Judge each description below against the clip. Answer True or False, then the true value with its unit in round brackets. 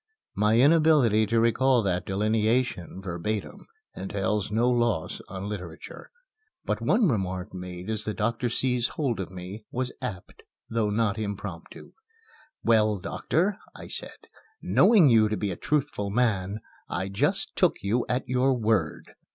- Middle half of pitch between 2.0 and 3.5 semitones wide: False (4.1 semitones)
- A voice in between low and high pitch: False (110 Hz)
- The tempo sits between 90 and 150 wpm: True (145 wpm)